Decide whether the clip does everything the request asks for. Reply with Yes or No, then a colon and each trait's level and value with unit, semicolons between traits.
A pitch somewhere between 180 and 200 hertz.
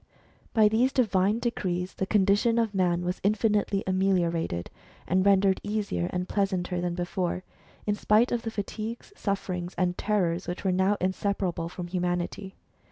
Yes: high, 190 Hz